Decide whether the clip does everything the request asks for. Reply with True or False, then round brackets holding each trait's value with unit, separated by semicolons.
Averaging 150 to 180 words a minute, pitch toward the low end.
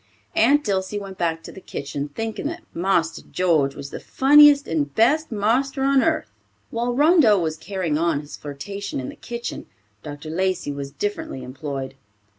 False (165 wpm; 190 Hz)